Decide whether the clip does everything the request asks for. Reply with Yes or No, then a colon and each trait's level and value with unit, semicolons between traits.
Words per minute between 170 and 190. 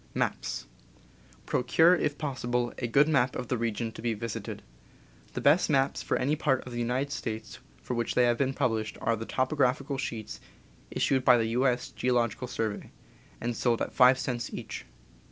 Yes: average, 185 wpm